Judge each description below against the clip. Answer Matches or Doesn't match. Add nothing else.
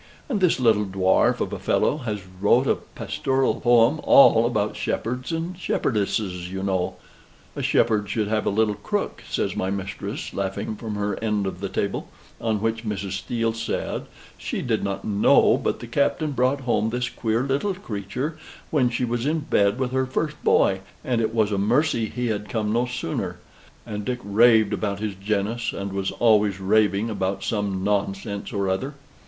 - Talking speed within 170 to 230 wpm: Matches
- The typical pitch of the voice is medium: Doesn't match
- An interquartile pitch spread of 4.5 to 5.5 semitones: Doesn't match